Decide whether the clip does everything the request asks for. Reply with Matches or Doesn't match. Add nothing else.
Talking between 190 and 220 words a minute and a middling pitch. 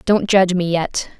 Matches